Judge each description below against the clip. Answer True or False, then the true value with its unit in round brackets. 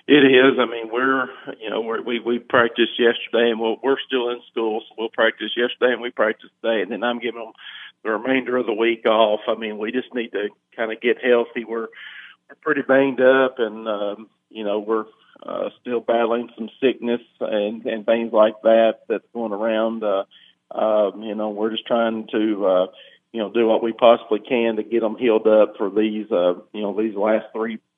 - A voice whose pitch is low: True (115 Hz)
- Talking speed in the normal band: False (215 wpm)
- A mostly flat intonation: True (1.7 semitones)